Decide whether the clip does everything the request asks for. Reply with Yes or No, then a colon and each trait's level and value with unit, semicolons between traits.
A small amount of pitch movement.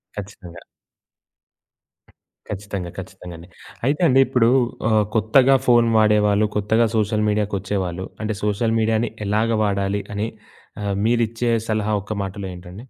Yes: narrow, 2.2 semitones